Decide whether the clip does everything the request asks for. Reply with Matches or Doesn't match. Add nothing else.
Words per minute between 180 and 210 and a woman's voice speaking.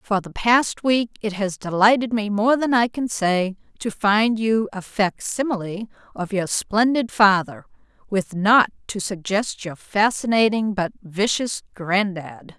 Doesn't match